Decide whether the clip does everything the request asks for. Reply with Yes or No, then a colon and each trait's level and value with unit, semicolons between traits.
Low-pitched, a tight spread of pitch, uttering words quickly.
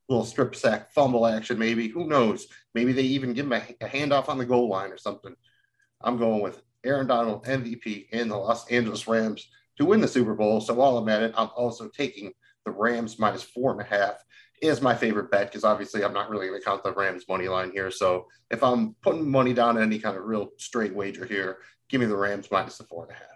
No: low, 115 Hz; average, 3.7 semitones; fast, 240 wpm